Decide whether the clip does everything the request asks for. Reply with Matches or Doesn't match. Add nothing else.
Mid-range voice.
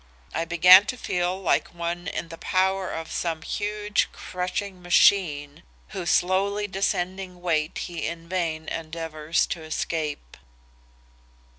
Matches